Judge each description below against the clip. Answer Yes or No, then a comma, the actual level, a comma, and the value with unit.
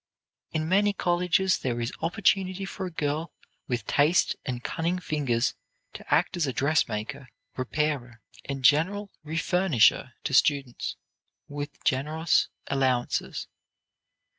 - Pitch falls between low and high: Yes, medium, 150 Hz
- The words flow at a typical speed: No, slow, 115 wpm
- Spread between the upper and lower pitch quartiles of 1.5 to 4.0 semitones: No, average, 5.2 semitones